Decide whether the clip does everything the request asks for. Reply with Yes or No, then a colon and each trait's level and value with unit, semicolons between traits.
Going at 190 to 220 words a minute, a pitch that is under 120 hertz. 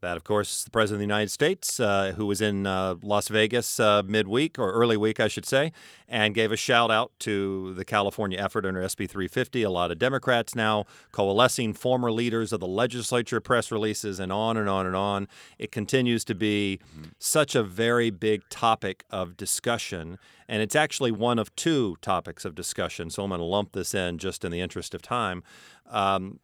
Yes: average, 200 wpm; low, 105 Hz